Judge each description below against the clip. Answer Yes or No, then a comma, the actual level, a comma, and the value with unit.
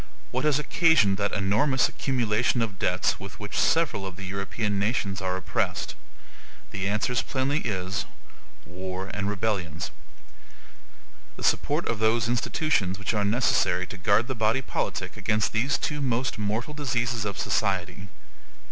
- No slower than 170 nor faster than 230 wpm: No, average, 145 wpm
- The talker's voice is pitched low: Yes, low, 105 Hz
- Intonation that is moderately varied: Yes, average, 4.0 semitones